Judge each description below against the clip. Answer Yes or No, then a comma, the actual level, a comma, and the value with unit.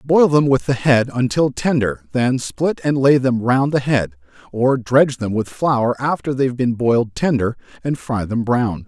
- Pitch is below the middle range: Yes, low, 125 Hz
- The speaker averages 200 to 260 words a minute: Yes, fast, 205 wpm